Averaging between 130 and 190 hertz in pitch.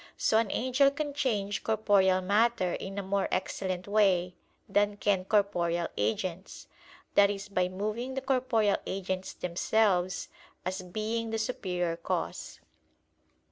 No: high, 200 Hz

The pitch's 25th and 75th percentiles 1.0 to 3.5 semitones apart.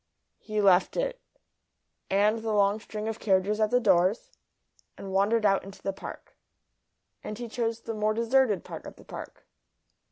Yes: narrow, 2.5 semitones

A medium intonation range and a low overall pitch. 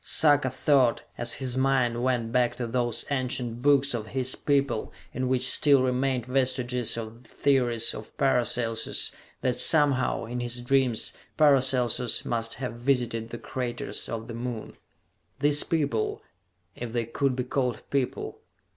No: narrow, 2.1 semitones; low, 125 Hz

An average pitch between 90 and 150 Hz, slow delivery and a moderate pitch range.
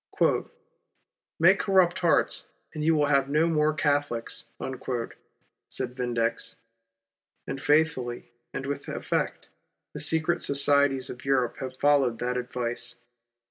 Yes: medium, 140 Hz; slow, 120 wpm; average, 3.3 semitones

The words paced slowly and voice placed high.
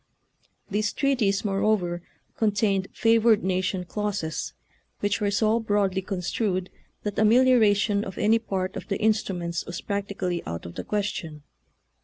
Yes: slow, 130 wpm; high, 200 Hz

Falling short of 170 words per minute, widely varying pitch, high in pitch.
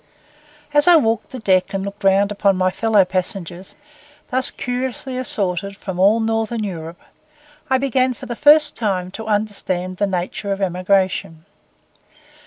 No: average, 150 wpm; average, 3.7 semitones; high, 200 Hz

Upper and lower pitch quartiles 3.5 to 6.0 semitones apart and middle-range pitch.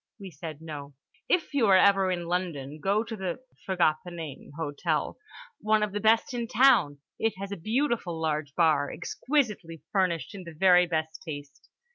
Yes: average, 5.2 semitones; medium, 180 Hz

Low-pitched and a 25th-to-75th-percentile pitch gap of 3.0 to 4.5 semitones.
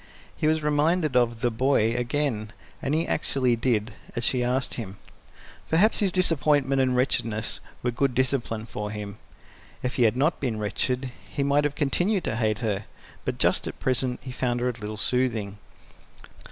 Yes: low, 125 Hz; average, 3.9 semitones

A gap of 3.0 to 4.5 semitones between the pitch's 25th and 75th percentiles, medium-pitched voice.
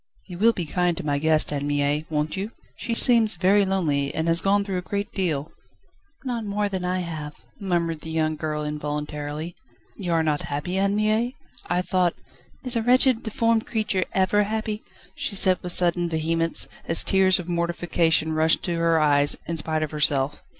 Yes: average, 4.2 semitones; medium, 175 Hz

